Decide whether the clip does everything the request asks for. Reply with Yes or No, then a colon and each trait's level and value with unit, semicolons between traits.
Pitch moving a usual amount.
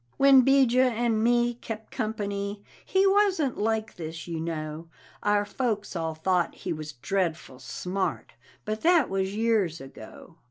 No: wide, 6.3 semitones